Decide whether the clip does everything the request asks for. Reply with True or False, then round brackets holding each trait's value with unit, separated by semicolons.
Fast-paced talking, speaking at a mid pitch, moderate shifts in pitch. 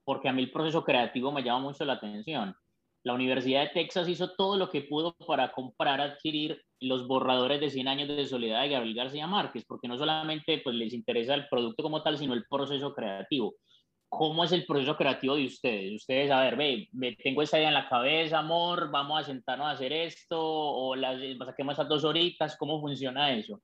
True (210 wpm; 145 Hz; 3.2 semitones)